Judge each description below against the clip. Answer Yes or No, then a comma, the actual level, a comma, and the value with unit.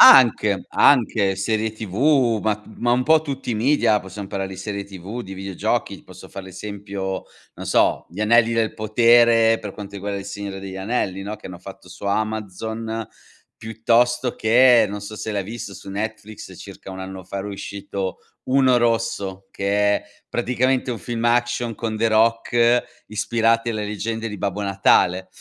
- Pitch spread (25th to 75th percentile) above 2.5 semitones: Yes, average, 2.9 semitones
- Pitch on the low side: Yes, low, 110 Hz